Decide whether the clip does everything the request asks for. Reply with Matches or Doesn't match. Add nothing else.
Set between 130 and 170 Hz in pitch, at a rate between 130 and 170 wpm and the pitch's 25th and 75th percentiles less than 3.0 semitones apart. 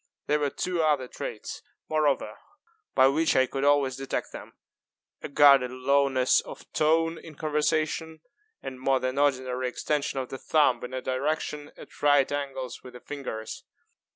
Matches